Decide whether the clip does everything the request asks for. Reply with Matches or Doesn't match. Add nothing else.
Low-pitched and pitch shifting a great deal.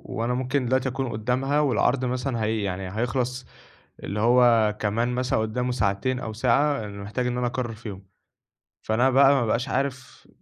Doesn't match